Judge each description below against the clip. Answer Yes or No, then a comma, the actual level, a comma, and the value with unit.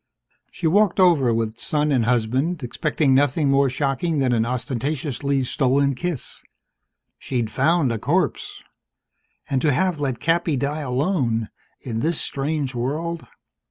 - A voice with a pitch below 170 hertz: Yes, medium, 140 Hz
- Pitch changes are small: No, average, 3.9 semitones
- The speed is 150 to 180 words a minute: No, slow, 135 wpm